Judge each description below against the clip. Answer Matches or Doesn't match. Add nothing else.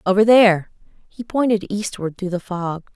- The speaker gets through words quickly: Doesn't match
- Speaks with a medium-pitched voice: Doesn't match